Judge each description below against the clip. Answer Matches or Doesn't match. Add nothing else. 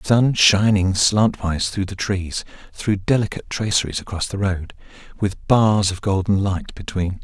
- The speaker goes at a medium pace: Matches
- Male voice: Matches